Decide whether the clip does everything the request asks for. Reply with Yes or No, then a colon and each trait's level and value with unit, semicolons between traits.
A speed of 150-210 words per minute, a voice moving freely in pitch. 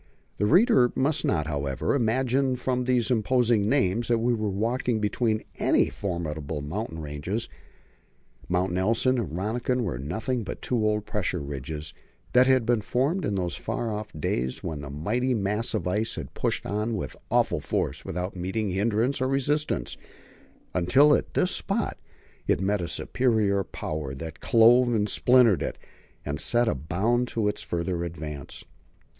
Yes: average, 160 wpm; wide, 5.9 semitones